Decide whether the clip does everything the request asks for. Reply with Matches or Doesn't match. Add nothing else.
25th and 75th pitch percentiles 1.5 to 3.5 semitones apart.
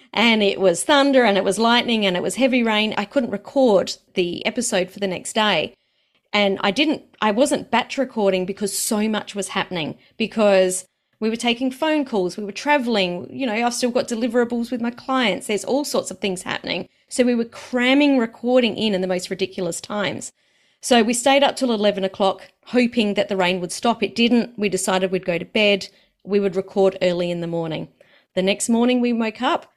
Doesn't match